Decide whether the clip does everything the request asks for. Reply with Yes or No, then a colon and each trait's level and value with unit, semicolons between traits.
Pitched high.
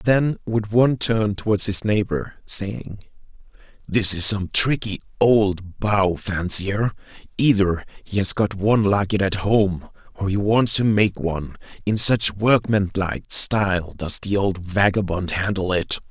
No: low, 100 Hz